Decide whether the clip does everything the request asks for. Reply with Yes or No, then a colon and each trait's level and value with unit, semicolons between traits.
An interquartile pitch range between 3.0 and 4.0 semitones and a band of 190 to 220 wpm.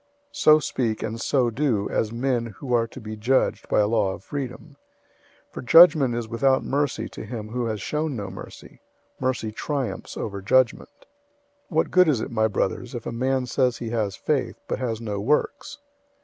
Yes: average, 3.6 semitones; average, 195 wpm